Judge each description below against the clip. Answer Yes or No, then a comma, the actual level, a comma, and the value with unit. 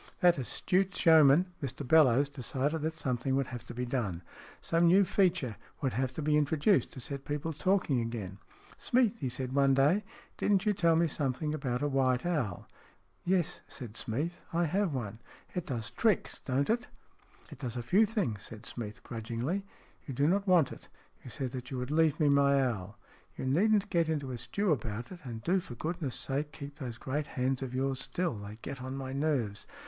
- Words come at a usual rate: No, fast, 220 wpm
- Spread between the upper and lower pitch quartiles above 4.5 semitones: Yes, average, 5.0 semitones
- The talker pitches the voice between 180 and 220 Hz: No, medium, 140 Hz